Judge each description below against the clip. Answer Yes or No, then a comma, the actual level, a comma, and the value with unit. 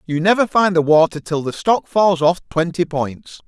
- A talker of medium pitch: Yes, medium, 170 Hz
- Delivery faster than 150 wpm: Yes, fast, 205 wpm